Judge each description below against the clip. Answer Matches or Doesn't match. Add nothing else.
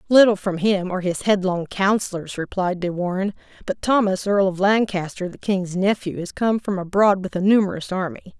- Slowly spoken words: Doesn't match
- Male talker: Doesn't match